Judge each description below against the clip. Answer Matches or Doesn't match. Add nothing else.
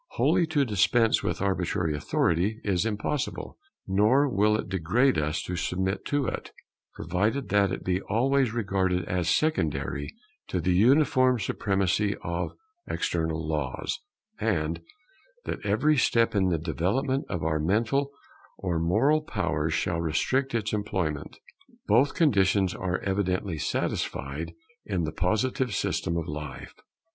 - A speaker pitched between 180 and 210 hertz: Doesn't match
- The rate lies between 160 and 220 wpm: Doesn't match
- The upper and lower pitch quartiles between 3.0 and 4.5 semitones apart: Doesn't match